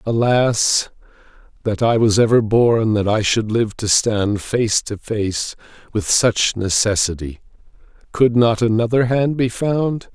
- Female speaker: No, male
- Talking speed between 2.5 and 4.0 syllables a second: Yes, 3.8 syllables/s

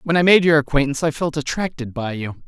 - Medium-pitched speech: Yes, medium, 145 Hz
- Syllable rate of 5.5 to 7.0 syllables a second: Yes, 6.4 syllables/s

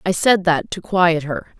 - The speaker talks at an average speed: No, fast, 225 wpm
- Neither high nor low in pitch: Yes, medium, 175 Hz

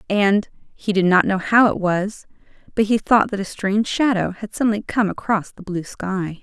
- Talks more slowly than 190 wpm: No, fast, 205 wpm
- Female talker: Yes, female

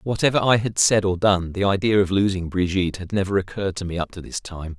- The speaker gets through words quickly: Yes, fast, 250 wpm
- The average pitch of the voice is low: Yes, very low, 95 Hz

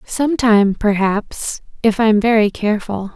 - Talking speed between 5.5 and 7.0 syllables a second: No, 4.6 syllables/s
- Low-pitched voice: No, high, 215 Hz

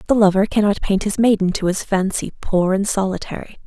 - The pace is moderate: Yes, average, 195 wpm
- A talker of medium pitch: No, high, 200 Hz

